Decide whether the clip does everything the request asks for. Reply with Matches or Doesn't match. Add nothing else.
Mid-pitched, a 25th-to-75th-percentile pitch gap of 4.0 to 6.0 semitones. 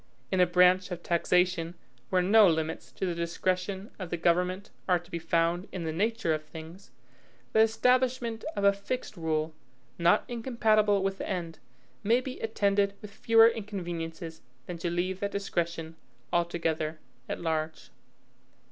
Doesn't match